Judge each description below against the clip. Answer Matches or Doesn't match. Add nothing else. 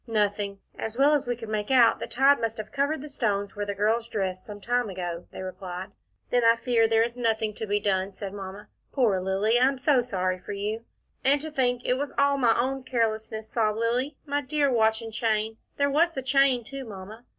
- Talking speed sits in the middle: Doesn't match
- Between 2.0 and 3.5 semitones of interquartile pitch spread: Doesn't match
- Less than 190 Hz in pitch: Doesn't match